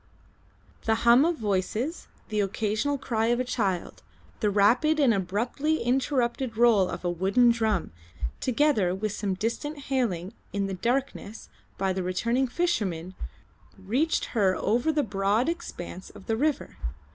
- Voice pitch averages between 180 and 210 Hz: No, high, 225 Hz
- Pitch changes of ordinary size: Yes, average, 5.0 semitones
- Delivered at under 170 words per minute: Yes, average, 145 wpm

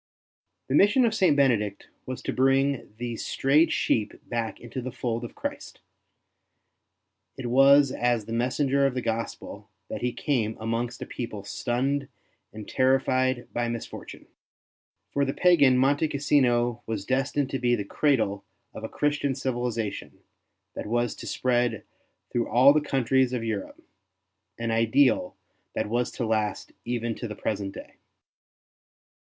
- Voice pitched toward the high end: No, low, 125 Hz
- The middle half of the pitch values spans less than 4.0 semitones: Yes, average, 2.9 semitones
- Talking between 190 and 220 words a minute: No, average, 150 wpm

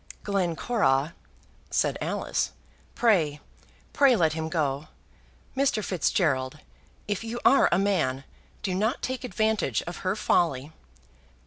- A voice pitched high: No, medium, 180 Hz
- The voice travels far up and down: Yes, wide, 6.2 semitones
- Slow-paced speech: Yes, slow, 115 wpm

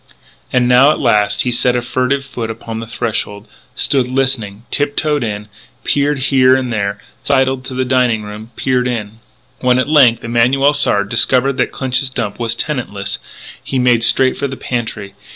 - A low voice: Yes, low, 125 Hz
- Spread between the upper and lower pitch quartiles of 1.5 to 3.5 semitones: Yes, average, 2.8 semitones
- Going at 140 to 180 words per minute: Yes, average, 175 wpm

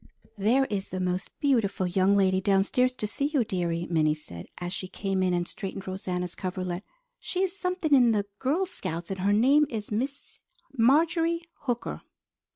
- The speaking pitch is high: Yes, high, 200 Hz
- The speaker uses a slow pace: No, average, 170 wpm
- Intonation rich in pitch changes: Yes, wide, 6.6 semitones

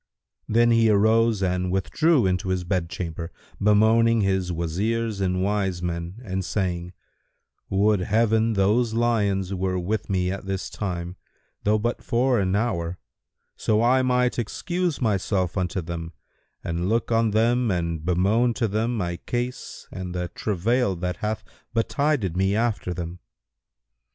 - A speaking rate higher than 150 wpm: No, average, 140 wpm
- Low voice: Yes, low, 100 Hz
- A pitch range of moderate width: Yes, average, 4.1 semitones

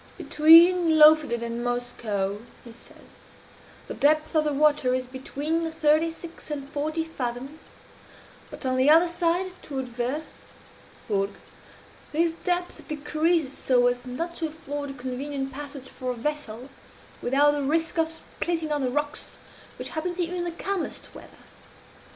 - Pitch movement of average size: Yes, average, 4.0 semitones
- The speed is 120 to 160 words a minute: Yes, average, 150 wpm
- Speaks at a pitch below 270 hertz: No, very high, 295 Hz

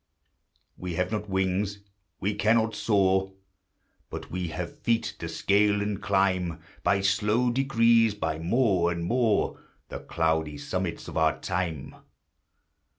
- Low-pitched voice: Yes, very low, 95 Hz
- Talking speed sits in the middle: No, slow, 130 wpm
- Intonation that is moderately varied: Yes, average, 3.7 semitones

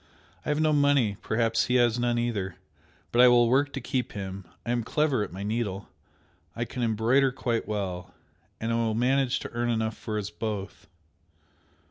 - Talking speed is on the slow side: No, average, 185 wpm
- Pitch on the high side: No, low, 115 Hz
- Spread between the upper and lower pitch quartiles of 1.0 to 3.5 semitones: Yes, average, 2.9 semitones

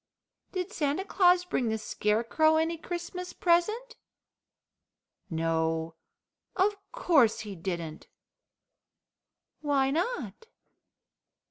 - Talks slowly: Yes, slow, 85 wpm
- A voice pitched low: No, very high, 315 Hz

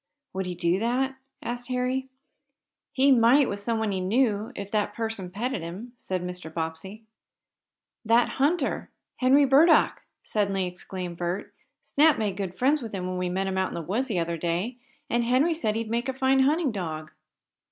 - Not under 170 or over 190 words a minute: Yes, average, 180 wpm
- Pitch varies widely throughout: Yes, wide, 5.7 semitones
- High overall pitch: Yes, high, 220 Hz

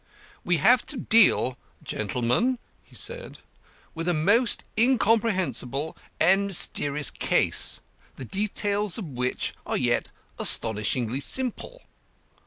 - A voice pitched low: No, medium, 185 Hz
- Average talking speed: No, slow, 105 wpm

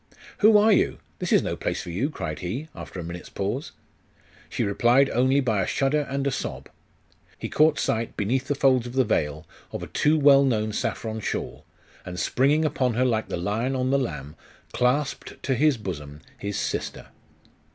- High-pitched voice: No, low, 125 Hz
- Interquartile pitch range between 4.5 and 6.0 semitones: Yes, wide, 5.5 semitones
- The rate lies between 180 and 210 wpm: Yes, average, 190 wpm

